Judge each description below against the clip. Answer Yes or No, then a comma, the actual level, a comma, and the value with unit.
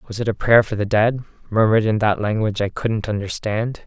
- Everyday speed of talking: No, fast, 215 wpm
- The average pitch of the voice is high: No, low, 110 Hz